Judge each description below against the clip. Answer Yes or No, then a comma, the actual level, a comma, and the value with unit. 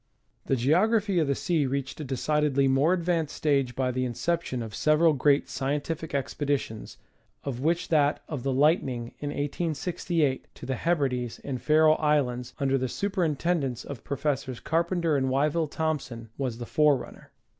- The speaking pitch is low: No, medium, 145 Hz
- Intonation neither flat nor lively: Yes, average, 3.4 semitones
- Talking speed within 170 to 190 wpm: No, average, 155 wpm